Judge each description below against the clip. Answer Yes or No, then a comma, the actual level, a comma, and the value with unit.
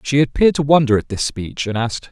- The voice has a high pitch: No, low, 130 Hz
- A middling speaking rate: No, fast, 255 wpm